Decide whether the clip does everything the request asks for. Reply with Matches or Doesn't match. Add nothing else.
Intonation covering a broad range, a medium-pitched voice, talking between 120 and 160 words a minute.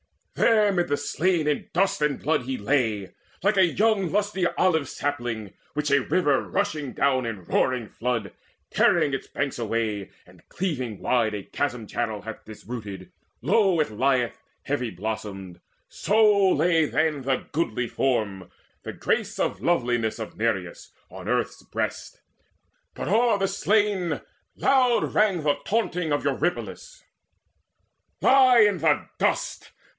Matches